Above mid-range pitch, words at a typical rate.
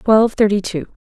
Yes: high, 205 Hz; average, 165 wpm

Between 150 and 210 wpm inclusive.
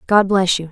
No: fast, 250 wpm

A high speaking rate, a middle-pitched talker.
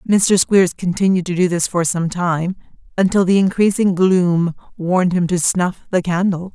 No: average, 175 wpm; medium, 180 Hz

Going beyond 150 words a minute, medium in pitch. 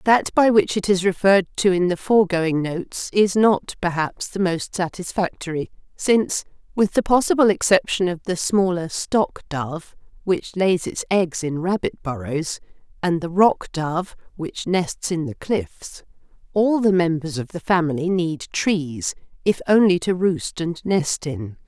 Yes: average, 160 wpm; medium, 175 Hz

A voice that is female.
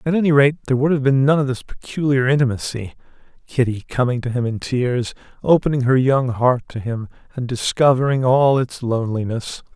No: male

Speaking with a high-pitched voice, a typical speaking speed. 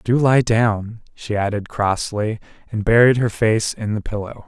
No: low, 110 Hz; average, 175 wpm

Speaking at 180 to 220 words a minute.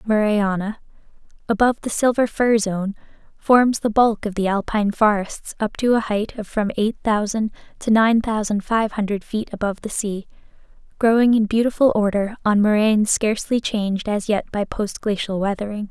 No: average, 165 wpm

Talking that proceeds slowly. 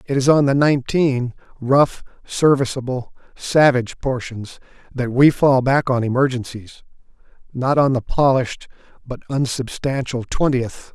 Yes: slow, 120 wpm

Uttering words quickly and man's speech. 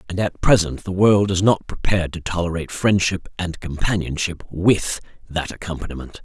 No: average, 155 wpm; male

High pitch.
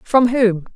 Yes: high, 225 Hz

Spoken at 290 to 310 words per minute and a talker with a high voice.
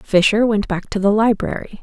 No: average, 200 wpm; high, 210 Hz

